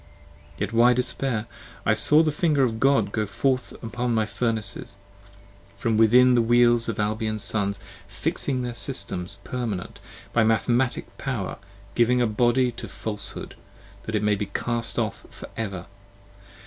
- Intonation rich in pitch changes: No, average, 2.7 semitones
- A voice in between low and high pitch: No, low, 115 Hz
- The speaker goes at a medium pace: Yes, average, 150 wpm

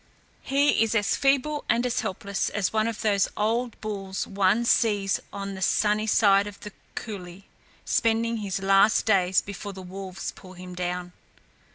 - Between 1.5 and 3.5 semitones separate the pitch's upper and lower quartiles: Yes, narrow, 2.6 semitones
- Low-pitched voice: No, high, 205 Hz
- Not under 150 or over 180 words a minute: Yes, average, 165 wpm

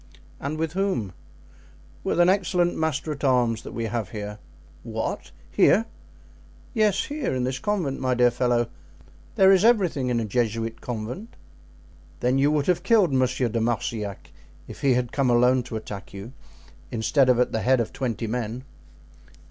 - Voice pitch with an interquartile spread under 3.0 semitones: No, wide, 5.5 semitones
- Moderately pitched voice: No, low, 125 Hz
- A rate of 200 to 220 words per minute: No, average, 165 wpm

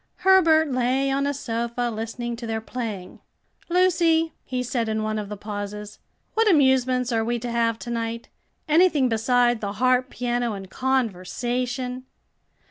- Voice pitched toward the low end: No, high, 245 Hz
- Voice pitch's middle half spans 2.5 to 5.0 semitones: Yes, average, 2.8 semitones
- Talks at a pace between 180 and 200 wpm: No, average, 150 wpm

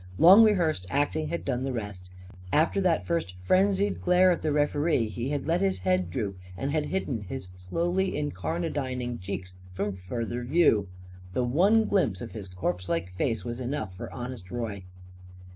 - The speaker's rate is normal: Yes, average, 170 wpm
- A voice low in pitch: Yes, low, 130 Hz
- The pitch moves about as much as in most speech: No, wide, 8.7 semitones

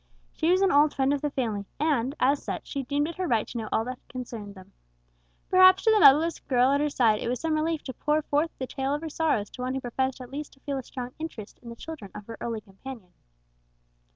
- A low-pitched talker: No, very high, 270 Hz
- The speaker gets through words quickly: Yes, fast, 255 wpm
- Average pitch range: Yes, average, 4.2 semitones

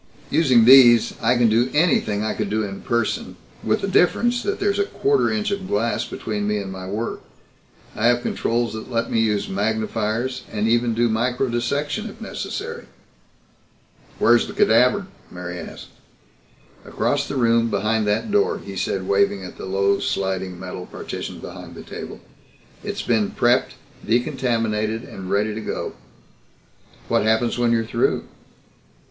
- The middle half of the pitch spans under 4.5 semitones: Yes, average, 3.0 semitones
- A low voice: Yes, low, 115 Hz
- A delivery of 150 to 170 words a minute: Yes, average, 155 wpm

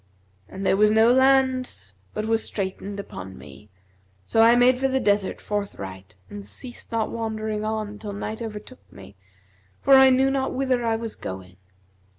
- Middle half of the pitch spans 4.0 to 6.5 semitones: Yes, average, 4.4 semitones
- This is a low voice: No, high, 220 Hz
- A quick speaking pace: No, average, 165 wpm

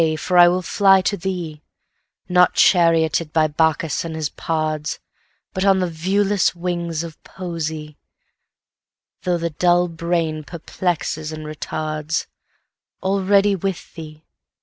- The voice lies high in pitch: No, medium, 170 Hz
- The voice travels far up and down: No, narrow, 2.6 semitones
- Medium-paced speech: No, slow, 105 wpm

